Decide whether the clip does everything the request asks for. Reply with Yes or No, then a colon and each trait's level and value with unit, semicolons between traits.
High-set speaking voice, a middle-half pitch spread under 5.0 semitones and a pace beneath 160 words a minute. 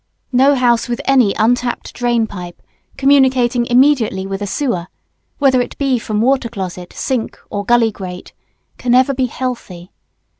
Yes: high, 240 Hz; average, 4.1 semitones; average, 150 wpm